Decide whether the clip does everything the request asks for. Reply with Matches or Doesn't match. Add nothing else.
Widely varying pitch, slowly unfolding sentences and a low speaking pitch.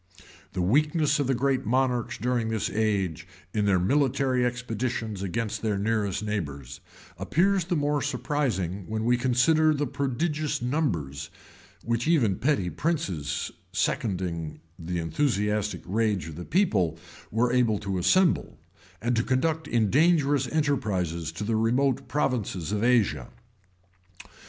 Matches